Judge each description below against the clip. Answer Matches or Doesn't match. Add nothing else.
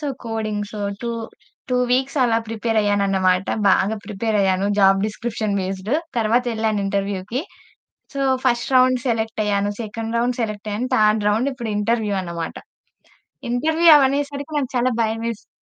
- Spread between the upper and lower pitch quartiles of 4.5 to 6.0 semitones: Doesn't match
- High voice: Matches